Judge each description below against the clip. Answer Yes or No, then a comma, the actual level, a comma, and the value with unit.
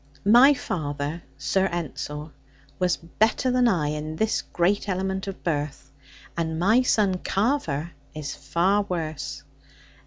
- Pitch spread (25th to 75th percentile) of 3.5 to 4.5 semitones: No, average, 5.0 semitones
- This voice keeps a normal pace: No, slow, 125 wpm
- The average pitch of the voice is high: No, medium, 175 Hz